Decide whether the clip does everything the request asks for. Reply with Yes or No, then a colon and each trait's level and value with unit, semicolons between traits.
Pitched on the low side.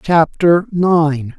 No: medium, 160 Hz